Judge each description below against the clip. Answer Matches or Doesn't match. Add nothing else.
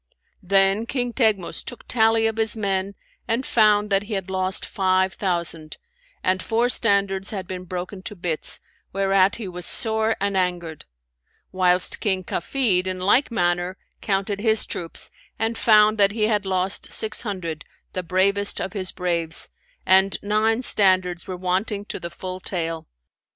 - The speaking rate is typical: Matches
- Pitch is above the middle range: Matches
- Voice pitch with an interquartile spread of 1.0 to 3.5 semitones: Matches